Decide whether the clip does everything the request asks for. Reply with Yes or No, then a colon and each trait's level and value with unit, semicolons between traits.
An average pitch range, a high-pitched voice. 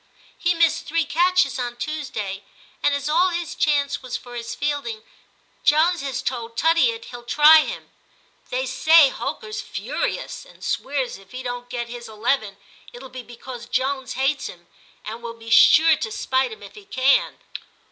Yes: average, 5.0 semitones; very high, 265 Hz